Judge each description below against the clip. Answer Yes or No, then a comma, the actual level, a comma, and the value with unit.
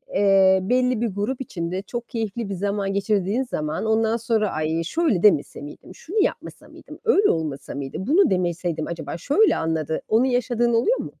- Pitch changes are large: Yes, wide, 5.9 semitones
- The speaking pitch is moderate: No, high, 205 Hz